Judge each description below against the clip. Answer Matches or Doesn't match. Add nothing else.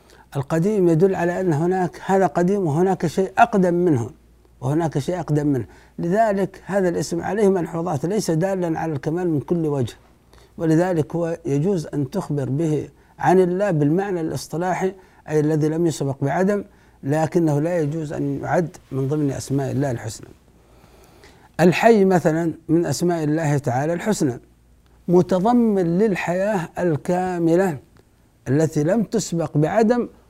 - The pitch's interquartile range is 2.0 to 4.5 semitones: Matches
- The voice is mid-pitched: Matches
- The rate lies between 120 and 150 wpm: Matches